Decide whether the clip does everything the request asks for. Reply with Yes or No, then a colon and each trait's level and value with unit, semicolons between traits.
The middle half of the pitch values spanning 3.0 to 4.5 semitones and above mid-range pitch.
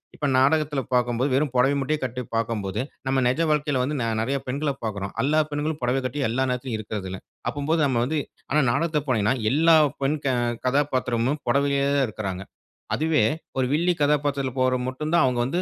No: average, 3.3 semitones; low, 135 Hz